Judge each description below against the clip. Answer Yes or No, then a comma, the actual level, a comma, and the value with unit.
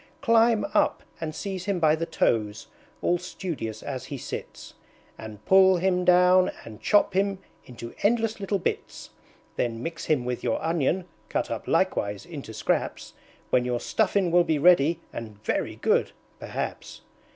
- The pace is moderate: Yes, average, 155 wpm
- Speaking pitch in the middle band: Yes, medium, 170 Hz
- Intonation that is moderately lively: No, wide, 7.3 semitones